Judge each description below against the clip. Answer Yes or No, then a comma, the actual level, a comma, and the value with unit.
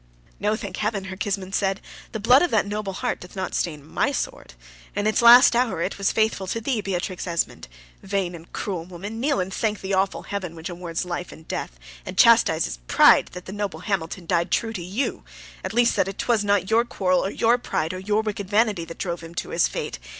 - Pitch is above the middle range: Yes, high, 195 Hz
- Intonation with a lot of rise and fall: No, average, 3.1 semitones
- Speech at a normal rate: No, fast, 220 wpm